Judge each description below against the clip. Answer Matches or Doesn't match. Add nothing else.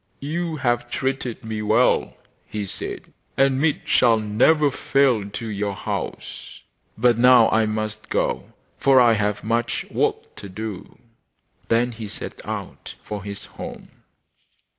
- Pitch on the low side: Matches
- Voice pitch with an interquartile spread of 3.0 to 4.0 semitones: Matches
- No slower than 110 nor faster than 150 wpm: Matches